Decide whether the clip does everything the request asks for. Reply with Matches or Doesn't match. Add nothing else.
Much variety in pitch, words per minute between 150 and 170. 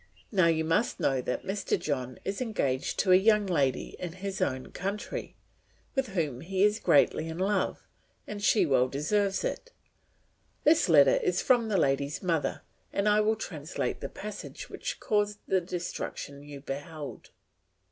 Matches